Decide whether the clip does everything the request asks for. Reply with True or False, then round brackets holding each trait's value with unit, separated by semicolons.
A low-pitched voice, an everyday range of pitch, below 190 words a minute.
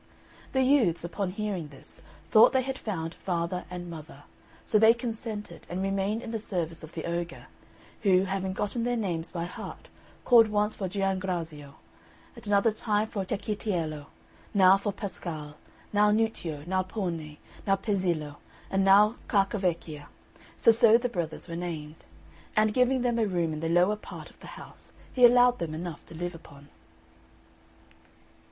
False (190 Hz; 4.2 semitones; 160 wpm)